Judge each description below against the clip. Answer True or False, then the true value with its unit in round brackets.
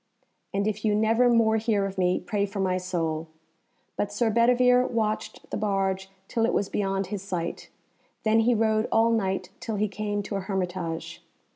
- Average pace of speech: True (180 wpm)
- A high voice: True (205 Hz)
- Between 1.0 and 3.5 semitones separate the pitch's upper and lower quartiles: True (2.6 semitones)